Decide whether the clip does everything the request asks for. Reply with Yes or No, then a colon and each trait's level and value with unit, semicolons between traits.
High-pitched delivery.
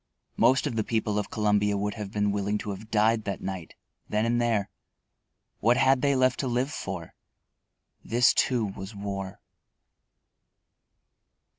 No: low, 105 Hz